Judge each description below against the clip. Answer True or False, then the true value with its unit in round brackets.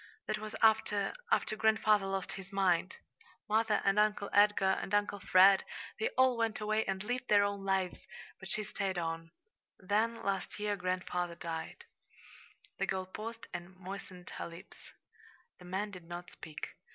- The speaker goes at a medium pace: True (160 wpm)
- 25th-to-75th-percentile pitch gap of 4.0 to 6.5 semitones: False (2.6 semitones)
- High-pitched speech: True (195 Hz)